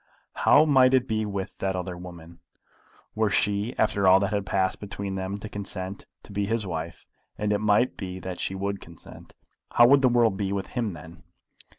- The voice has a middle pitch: No, low, 100 Hz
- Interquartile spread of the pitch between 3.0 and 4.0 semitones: No, narrow, 2.5 semitones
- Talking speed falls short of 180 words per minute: No, fast, 205 wpm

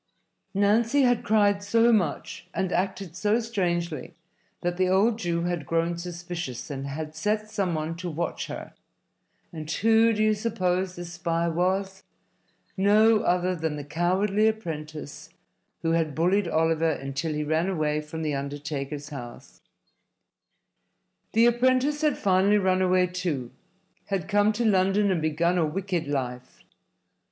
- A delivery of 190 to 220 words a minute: No, average, 145 wpm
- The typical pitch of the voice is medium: Yes, medium, 180 Hz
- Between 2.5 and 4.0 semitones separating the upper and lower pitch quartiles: No, average, 4.4 semitones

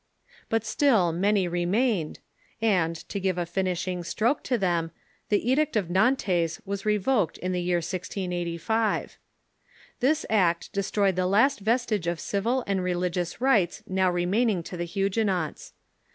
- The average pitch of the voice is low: No, high, 190 Hz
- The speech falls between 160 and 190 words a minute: No, average, 145 wpm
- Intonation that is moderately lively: Yes, average, 3.9 semitones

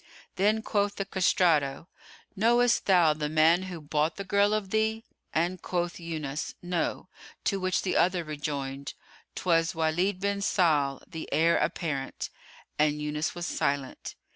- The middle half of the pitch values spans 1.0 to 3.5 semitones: No, average, 4.1 semitones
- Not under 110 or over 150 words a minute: Yes, average, 140 wpm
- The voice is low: No, medium, 170 Hz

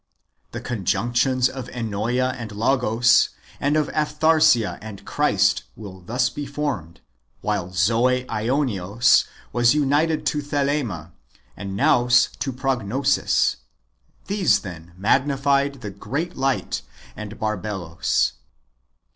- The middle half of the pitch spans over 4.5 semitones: Yes, average, 5.0 semitones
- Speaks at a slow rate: Yes, slow, 105 wpm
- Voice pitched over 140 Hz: No, low, 125 Hz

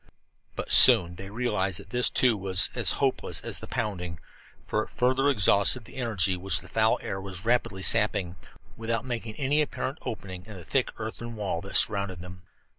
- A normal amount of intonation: Yes, average, 4.0 semitones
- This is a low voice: Yes, low, 105 Hz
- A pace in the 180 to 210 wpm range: Yes, average, 185 wpm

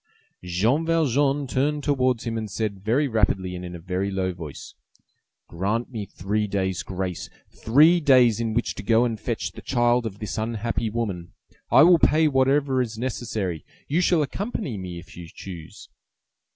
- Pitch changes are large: Yes, wide, 5.8 semitones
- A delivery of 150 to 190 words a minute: Yes, average, 170 wpm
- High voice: No, low, 115 Hz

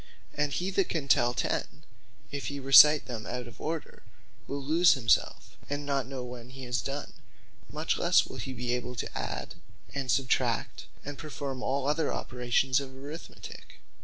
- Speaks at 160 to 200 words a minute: Yes, average, 170 wpm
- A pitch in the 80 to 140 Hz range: Yes, low, 135 Hz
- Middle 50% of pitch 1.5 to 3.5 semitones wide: Yes, average, 2.8 semitones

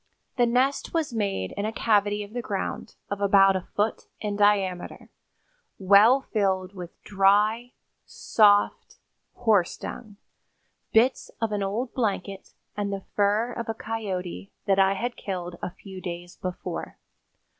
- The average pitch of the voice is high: Yes, high, 205 Hz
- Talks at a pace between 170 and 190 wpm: No, average, 145 wpm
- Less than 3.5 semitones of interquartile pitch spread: Yes, narrow, 2.6 semitones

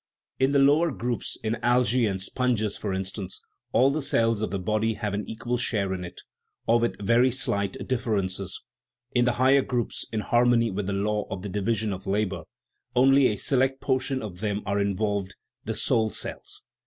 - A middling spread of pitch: Yes, average, 3.7 semitones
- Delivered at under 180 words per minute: No, average, 190 wpm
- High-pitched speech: No, low, 110 Hz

